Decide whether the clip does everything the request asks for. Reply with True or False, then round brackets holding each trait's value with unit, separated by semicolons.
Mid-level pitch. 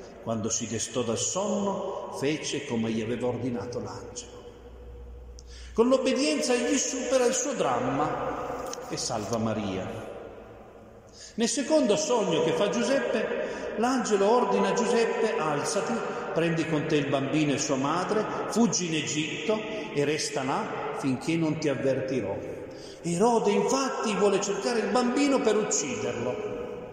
True (165 Hz)